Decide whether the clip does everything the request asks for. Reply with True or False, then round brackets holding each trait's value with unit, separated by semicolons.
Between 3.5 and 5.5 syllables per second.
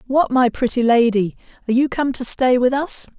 True (5.3 syllables/s)